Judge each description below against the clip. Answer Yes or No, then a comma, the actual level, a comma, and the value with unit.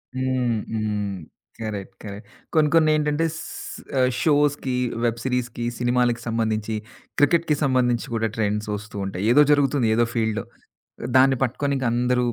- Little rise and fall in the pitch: No, average, 3.5 semitones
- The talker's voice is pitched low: Yes, low, 125 Hz